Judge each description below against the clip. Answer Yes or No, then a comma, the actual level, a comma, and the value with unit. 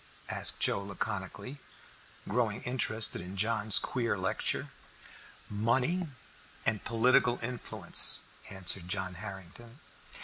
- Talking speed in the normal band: No, slow, 95 wpm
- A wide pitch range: No, average, 3.8 semitones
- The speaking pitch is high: No, low, 110 Hz